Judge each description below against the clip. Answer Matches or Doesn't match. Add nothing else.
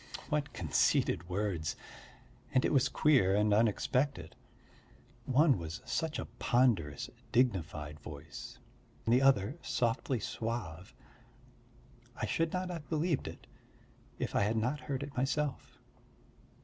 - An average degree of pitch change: Doesn't match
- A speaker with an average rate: Doesn't match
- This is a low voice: Matches